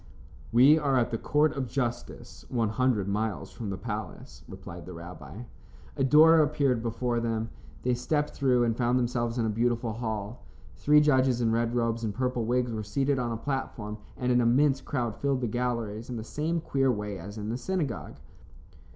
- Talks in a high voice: No, low, 120 Hz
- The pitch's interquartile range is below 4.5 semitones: Yes, average, 3.0 semitones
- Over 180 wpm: Yes, average, 190 wpm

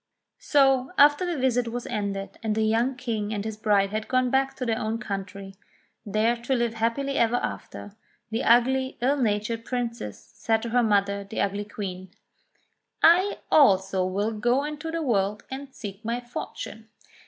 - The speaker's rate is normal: Yes, average, 175 wpm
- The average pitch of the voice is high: Yes, high, 230 Hz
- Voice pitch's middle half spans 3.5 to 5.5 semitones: Yes, average, 3.8 semitones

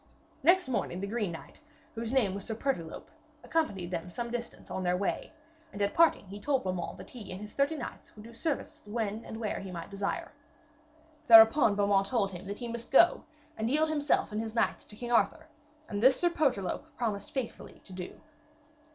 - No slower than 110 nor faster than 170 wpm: No, average, 200 wpm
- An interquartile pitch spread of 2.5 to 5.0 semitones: Yes, average, 4.4 semitones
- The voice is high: Yes, high, 220 Hz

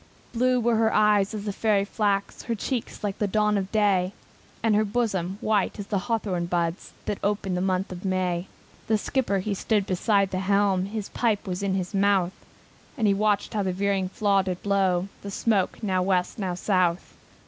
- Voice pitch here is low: No, high, 200 Hz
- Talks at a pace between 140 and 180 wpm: No, average, 200 wpm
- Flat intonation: Yes, narrow, 2.2 semitones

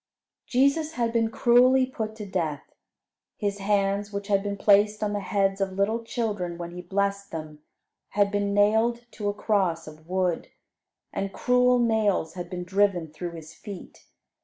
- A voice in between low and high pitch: No, high, 200 Hz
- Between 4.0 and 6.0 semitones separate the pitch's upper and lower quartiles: No, average, 3.4 semitones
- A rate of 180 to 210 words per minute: No, average, 165 wpm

